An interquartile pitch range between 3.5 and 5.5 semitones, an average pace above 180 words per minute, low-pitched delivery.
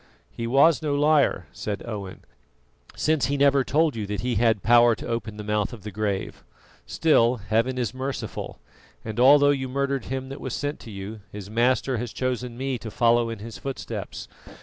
Yes: average, 3.9 semitones; average, 190 wpm; low, 120 Hz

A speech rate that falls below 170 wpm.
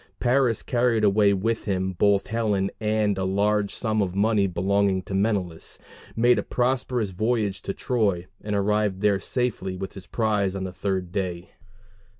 Yes: average, 160 wpm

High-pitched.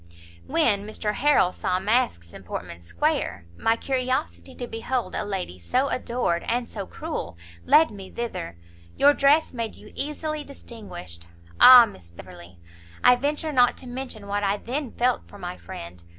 Yes: high, 215 Hz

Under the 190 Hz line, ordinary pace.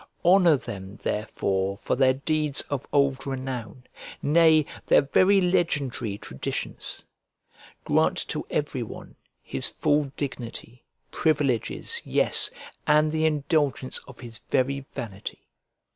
No: low, 135 Hz; slow, 115 wpm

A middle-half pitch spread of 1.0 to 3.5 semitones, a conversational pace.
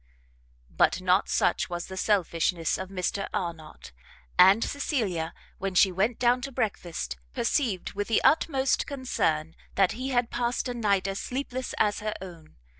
No: wide, 5.5 semitones; average, 155 wpm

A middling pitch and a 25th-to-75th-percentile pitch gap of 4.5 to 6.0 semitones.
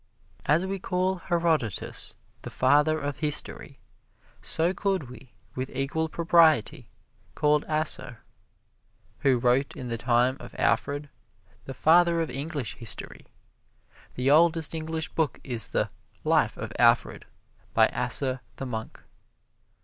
No: medium, 150 Hz; average, 4.1 semitones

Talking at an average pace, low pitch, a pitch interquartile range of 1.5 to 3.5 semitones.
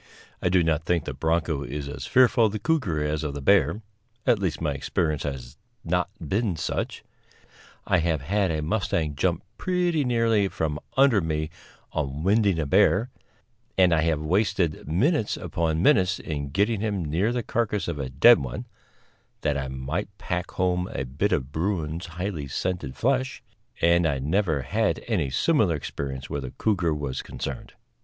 No: average, 170 wpm; very low, 85 Hz; wide, 5.4 semitones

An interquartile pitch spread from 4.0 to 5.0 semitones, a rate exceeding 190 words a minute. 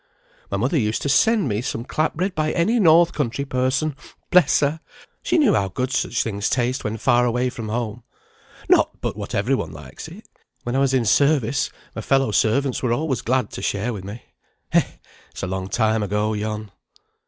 Yes: average, 4.7 semitones; average, 200 wpm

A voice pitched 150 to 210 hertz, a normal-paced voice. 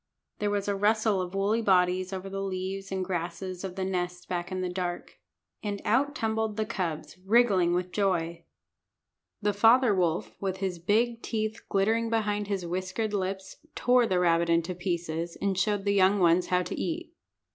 Yes: high, 190 Hz; average, 180 wpm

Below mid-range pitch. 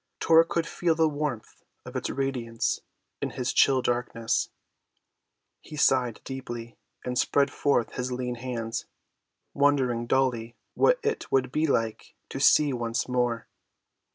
Yes: low, 125 Hz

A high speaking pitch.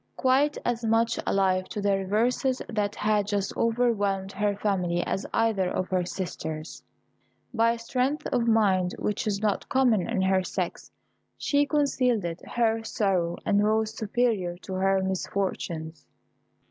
Yes: high, 205 Hz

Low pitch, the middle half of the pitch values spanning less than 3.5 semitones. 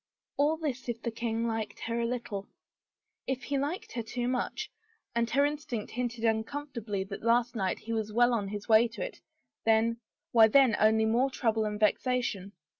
No: high, 235 Hz; narrow, 2.4 semitones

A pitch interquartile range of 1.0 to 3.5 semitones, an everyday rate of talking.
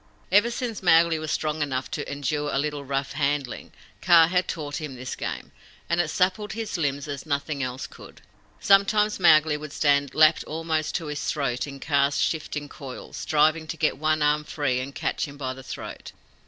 Yes: narrow, 2.5 semitones; average, 190 wpm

